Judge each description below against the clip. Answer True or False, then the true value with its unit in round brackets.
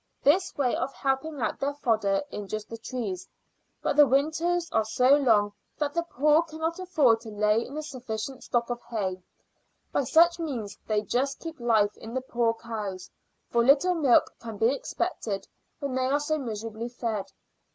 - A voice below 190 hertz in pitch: False (250 Hz)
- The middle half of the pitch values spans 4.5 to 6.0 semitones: True (5.0 semitones)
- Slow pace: False (175 wpm)